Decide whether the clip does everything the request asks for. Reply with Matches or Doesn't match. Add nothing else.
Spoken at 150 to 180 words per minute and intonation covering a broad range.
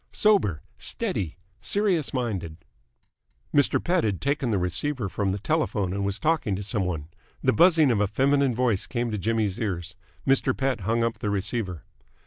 Matches